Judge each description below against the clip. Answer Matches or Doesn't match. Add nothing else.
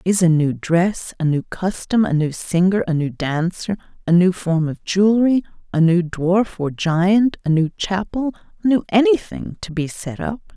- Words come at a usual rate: Matches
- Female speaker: Matches